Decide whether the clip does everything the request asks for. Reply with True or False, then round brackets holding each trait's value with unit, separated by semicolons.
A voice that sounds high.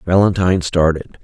False (90 Hz)